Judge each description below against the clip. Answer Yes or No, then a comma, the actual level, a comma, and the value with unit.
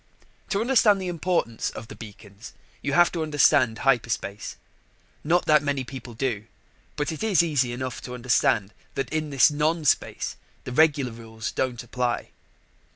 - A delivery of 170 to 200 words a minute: No, average, 160 wpm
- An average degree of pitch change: Yes, average, 5.0 semitones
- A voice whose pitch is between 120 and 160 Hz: Yes, low, 135 Hz